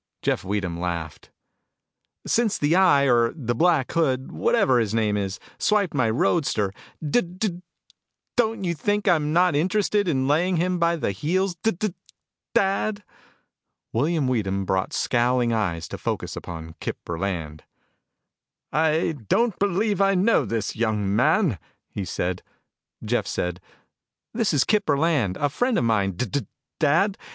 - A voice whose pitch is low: No, medium, 145 Hz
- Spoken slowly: No, average, 145 wpm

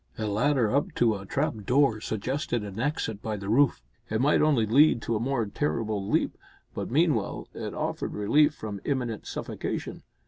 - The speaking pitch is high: No, low, 115 Hz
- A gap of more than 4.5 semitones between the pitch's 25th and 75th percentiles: Yes, average, 4.9 semitones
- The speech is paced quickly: No, average, 175 wpm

